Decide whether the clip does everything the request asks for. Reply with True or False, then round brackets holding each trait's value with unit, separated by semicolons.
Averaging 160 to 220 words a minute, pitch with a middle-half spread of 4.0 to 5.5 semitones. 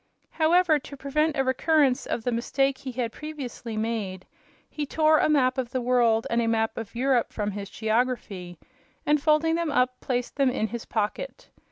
True (185 wpm; 4.4 semitones)